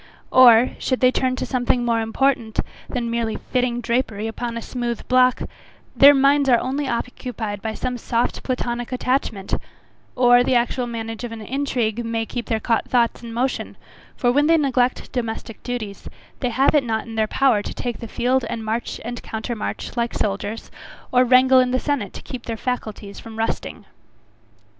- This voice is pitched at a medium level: No, high, 240 Hz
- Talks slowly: No, average, 180 wpm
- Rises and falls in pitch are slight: Yes, narrow, 2.1 semitones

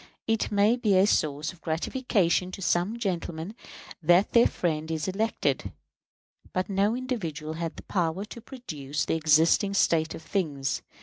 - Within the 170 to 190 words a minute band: No, average, 150 wpm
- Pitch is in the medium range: Yes, medium, 180 Hz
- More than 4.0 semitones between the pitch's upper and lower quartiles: Yes, average, 4.6 semitones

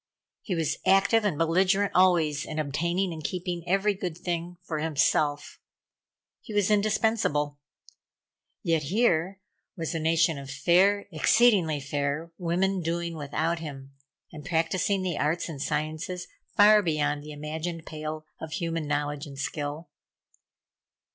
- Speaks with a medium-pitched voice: Yes, medium, 165 Hz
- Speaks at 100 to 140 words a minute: Yes, slow, 135 wpm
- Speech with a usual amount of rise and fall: Yes, average, 3.4 semitones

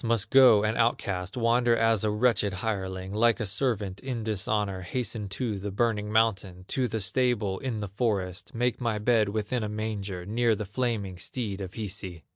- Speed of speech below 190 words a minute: Yes, average, 180 wpm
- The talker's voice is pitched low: Yes, low, 105 Hz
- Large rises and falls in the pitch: No, average, 3.0 semitones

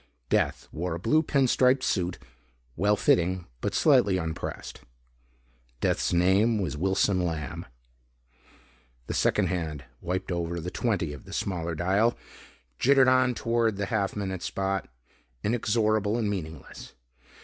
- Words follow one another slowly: Yes, slow, 130 wpm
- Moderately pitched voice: No, very low, 95 Hz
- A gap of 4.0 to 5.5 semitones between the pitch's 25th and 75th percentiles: Yes, average, 4.3 semitones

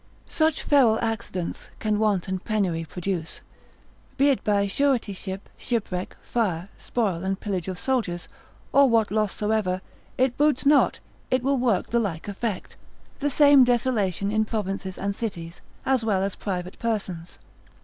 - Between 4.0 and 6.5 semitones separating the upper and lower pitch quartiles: Yes, average, 4.3 semitones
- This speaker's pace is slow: No, average, 150 wpm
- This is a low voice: No, high, 210 Hz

